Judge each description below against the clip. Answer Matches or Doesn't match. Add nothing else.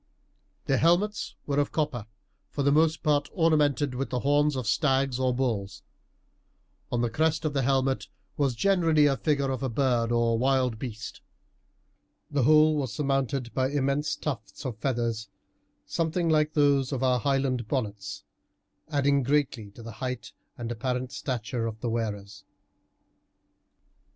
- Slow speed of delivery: Doesn't match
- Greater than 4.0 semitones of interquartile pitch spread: Doesn't match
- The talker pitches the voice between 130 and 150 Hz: Matches